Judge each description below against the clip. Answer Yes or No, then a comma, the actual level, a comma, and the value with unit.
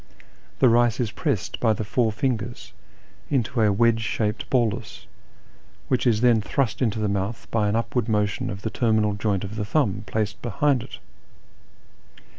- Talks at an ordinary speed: Yes, average, 165 wpm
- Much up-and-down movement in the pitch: No, narrow, 2.5 semitones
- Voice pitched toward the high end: No, low, 110 Hz